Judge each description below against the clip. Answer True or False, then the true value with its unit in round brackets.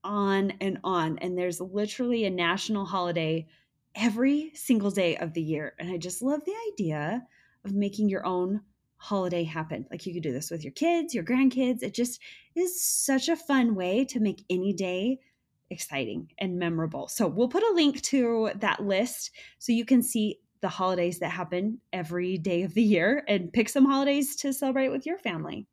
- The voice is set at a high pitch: True (205 Hz)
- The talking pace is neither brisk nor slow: True (190 wpm)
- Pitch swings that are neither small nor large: False (6.3 semitones)